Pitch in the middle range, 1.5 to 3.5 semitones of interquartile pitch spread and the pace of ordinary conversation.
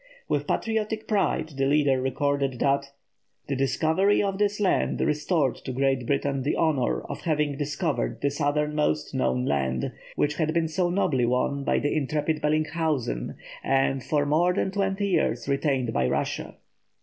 Yes: medium, 145 Hz; average, 3.2 semitones; average, 155 wpm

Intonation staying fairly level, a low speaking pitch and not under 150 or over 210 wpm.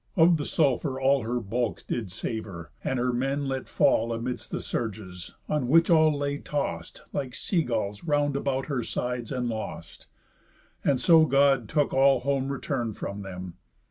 No: average, 3.9 semitones; low, 130 Hz; average, 170 wpm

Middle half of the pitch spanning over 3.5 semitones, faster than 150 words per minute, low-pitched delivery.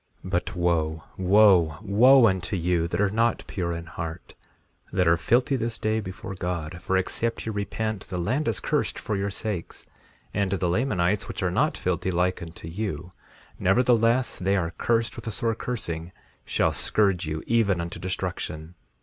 Yes: average, 4.1 semitones; average, 170 wpm; very low, 95 Hz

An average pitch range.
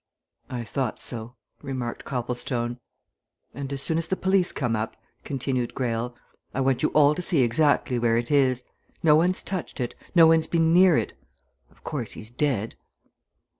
Yes: average, 4.7 semitones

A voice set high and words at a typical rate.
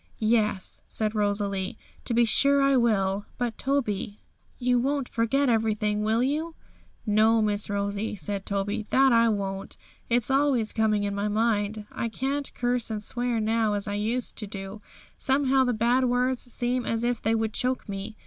Yes: high, 225 Hz; average, 170 wpm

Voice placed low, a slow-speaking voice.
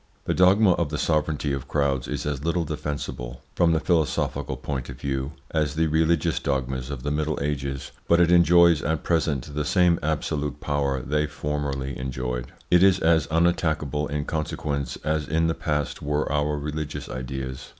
No: very low, 75 Hz; average, 170 wpm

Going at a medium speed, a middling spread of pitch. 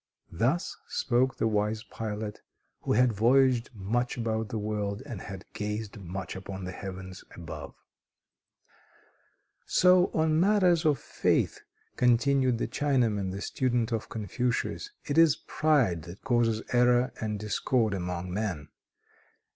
No: slow, 130 wpm; average, 4.1 semitones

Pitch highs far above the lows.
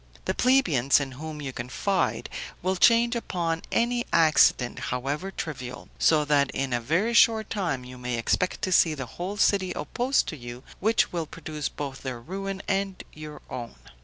Yes: wide, 6.7 semitones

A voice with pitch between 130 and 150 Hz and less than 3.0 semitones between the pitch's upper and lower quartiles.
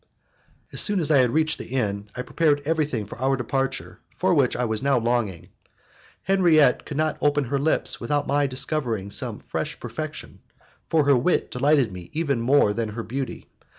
No: low, 135 Hz; average, 4.2 semitones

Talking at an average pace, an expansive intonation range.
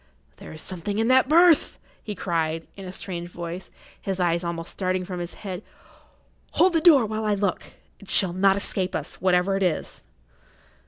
No: average, 175 wpm; average, 3.0 semitones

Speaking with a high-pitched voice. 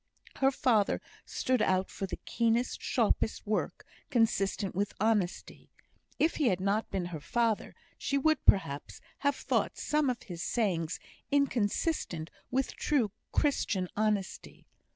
Yes: high, 215 Hz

